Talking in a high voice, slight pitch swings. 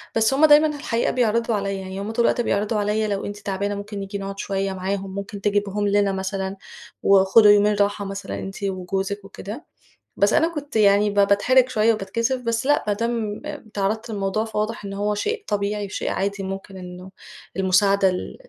Yes: high, 205 Hz; narrow, 1.9 semitones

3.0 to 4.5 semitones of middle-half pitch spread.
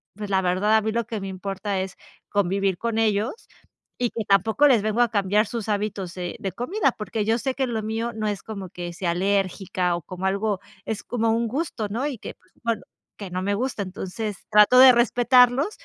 Yes: average, 3.3 semitones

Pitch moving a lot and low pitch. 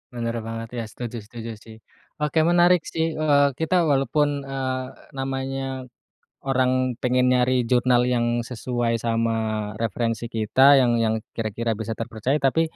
No: average, 2.8 semitones; low, 125 Hz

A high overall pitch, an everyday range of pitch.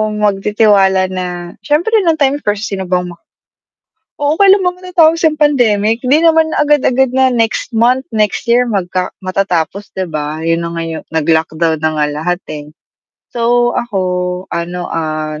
No: high, 205 Hz; wide, 7.4 semitones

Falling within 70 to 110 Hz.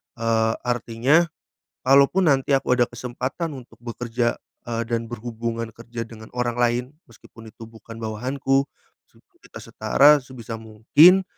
No: low, 120 Hz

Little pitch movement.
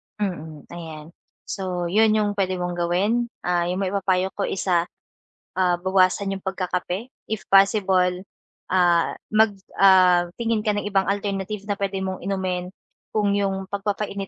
Yes: narrow, 2.0 semitones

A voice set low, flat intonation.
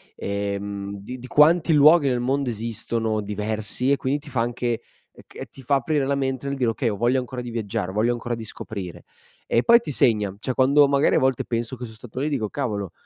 No: low, 120 Hz; average, 4.0 semitones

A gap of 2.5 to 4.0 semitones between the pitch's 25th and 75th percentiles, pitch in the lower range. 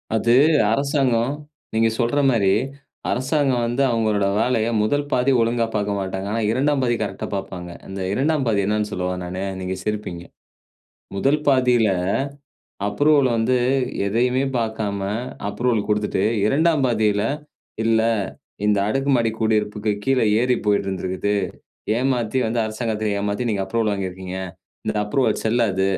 Yes: average, 3.6 semitones; low, 110 Hz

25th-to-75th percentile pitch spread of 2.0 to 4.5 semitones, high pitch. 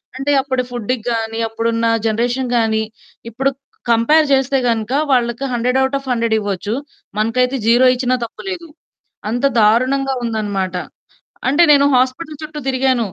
Yes: average, 2.9 semitones; high, 245 Hz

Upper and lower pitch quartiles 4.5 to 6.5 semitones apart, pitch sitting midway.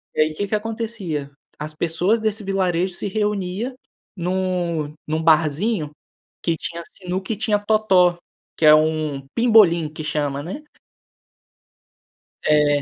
Yes: average, 5.0 semitones; medium, 175 Hz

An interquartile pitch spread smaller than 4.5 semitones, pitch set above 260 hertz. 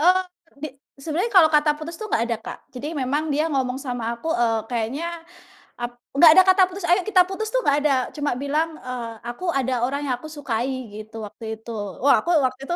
No: average, 5.2 semitones; very high, 285 Hz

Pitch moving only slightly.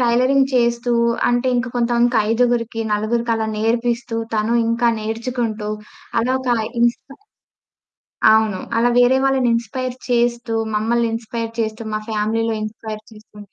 Yes: narrow, 1.7 semitones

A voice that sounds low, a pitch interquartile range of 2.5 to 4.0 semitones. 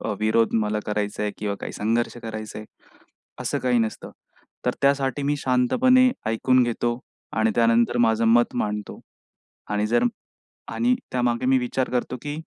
Yes: low, 120 Hz; average, 2.8 semitones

